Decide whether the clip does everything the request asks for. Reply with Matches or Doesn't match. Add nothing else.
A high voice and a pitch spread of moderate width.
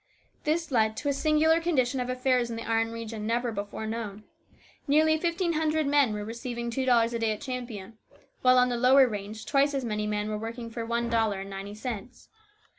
Matches